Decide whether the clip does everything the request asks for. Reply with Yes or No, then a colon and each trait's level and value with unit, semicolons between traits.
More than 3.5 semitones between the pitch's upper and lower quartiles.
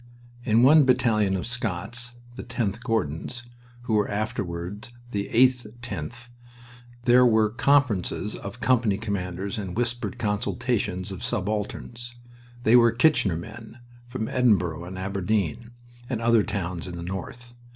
Yes: average, 3.9 semitones